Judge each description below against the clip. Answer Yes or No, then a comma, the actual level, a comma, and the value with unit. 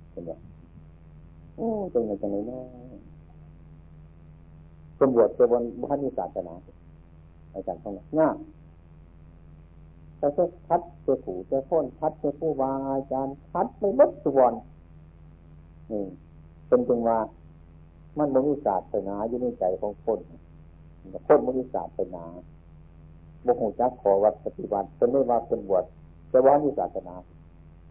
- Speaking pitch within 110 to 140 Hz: No, very low, 85 Hz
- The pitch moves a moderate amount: No, wide, 8.2 semitones